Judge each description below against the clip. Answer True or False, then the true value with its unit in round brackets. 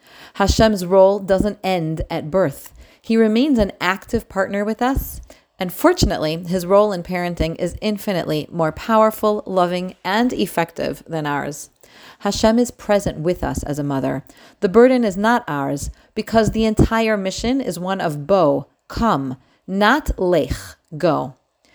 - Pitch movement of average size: True (4.5 semitones)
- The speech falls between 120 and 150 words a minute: True (145 wpm)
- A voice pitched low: False (195 Hz)